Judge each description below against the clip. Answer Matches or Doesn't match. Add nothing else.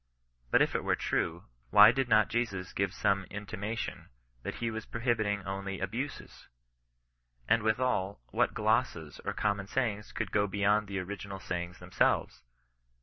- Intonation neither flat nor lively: Doesn't match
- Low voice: Matches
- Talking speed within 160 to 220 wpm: Doesn't match